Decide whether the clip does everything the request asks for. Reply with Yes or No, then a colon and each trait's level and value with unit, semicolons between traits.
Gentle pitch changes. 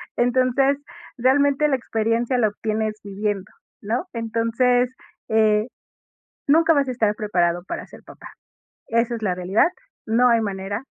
No: average, 3.1 semitones